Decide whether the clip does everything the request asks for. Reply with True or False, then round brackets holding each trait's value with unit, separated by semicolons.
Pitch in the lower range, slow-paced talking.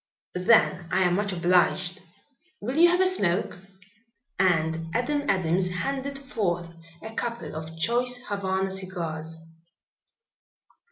False (190 Hz; 115 wpm)